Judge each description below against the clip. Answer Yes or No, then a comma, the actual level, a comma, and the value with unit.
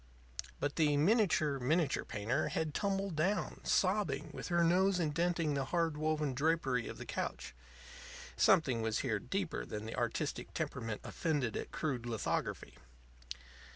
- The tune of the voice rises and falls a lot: No, average, 4.7 semitones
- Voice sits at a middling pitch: Yes, medium, 155 Hz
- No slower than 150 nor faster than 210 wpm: No, average, 140 wpm